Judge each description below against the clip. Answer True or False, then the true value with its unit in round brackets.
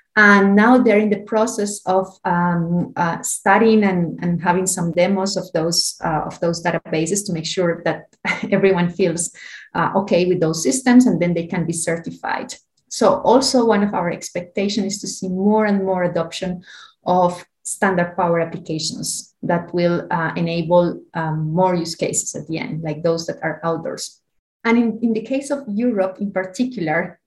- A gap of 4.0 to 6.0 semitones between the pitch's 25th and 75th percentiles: False (3.1 semitones)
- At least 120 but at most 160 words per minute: False (175 wpm)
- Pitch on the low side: False (180 Hz)